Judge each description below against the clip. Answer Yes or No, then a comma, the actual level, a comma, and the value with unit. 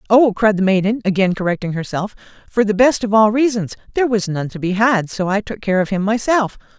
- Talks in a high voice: Yes, high, 210 Hz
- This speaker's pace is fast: Yes, fast, 230 wpm